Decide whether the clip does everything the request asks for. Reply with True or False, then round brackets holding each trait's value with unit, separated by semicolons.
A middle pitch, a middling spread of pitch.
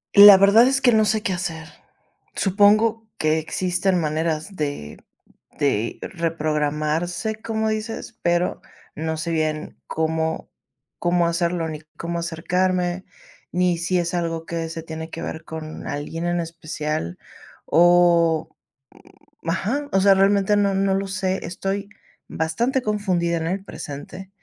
True (175 Hz; 3.5 semitones)